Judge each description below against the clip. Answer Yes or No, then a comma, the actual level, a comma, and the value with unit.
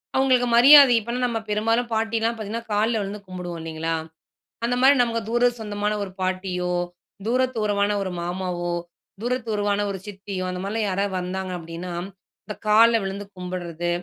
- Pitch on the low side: No, high, 205 Hz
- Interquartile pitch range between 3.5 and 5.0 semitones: Yes, average, 3.8 semitones